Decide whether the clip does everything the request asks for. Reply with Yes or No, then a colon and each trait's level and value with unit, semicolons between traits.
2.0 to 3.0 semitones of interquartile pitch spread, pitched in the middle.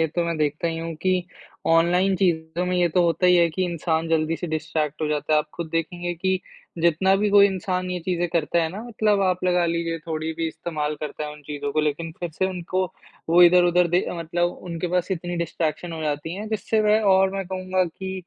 Yes: narrow, 2.4 semitones; medium, 170 Hz